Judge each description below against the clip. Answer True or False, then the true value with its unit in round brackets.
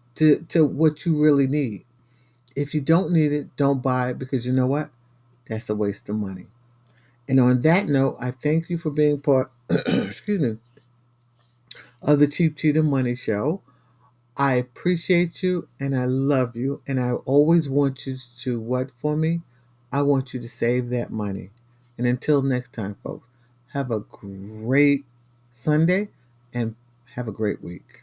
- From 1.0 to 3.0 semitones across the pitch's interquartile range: False (3.5 semitones)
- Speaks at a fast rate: False (165 wpm)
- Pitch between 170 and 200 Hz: False (130 Hz)